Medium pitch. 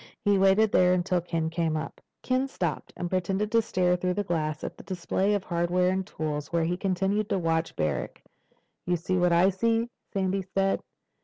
Yes: medium, 180 Hz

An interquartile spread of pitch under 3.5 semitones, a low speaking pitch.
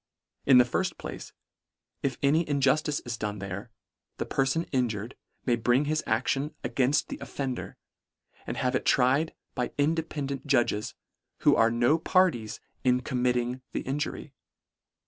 Yes: average, 3.0 semitones; low, 130 Hz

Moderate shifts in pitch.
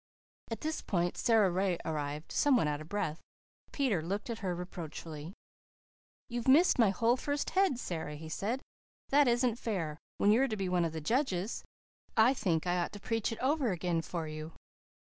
No: wide, 6.5 semitones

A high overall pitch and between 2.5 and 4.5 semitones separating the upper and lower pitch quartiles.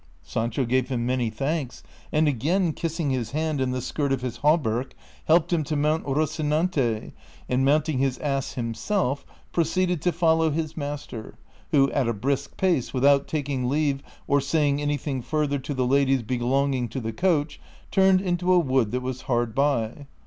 No: medium, 140 Hz; average, 3.6 semitones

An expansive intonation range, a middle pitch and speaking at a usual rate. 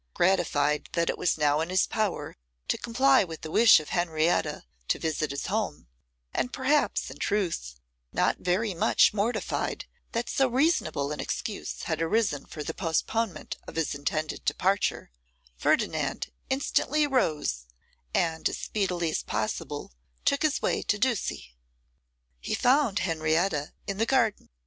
Yes: wide, 6.6 semitones; medium, 180 Hz; average, 145 wpm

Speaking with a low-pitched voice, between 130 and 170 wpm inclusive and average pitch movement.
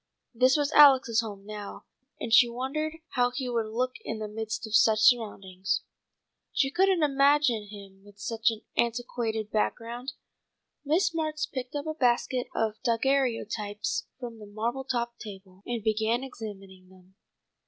No: high, 230 Hz; average, 150 wpm; average, 3.7 semitones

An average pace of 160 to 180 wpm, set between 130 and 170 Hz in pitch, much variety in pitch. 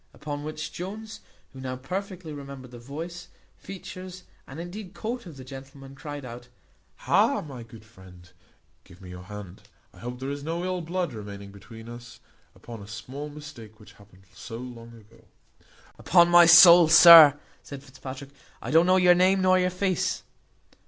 Yes: average, 170 wpm; medium, 140 Hz; wide, 6.9 semitones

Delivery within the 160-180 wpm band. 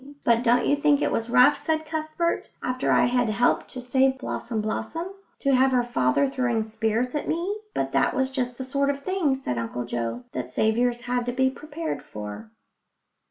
No: average, 195 wpm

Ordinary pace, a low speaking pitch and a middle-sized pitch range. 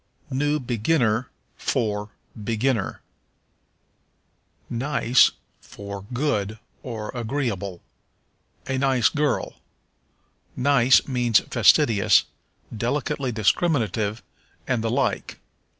No: slow, 75 wpm; low, 120 Hz; average, 3.9 semitones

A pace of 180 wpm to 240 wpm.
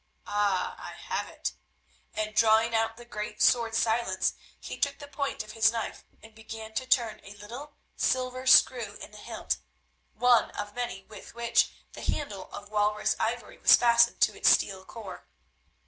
No: average, 170 wpm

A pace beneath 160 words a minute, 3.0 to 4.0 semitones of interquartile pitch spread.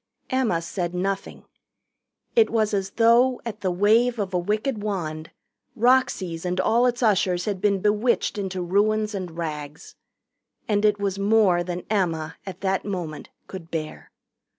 Yes: average, 150 wpm; average, 3.4 semitones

